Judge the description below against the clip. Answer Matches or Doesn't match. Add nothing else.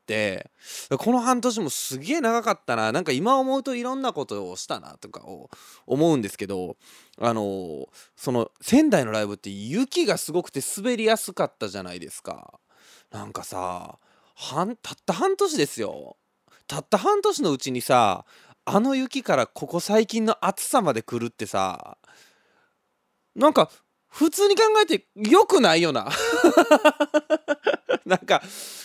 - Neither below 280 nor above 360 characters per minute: Matches